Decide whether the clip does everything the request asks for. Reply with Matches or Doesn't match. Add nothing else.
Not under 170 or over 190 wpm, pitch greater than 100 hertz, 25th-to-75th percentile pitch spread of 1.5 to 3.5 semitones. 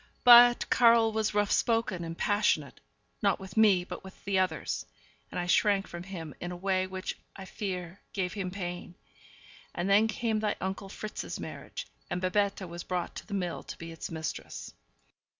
Matches